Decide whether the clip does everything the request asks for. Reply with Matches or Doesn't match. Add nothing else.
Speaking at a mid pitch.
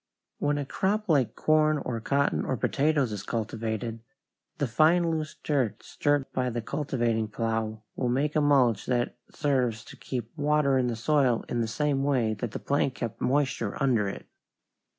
Doesn't match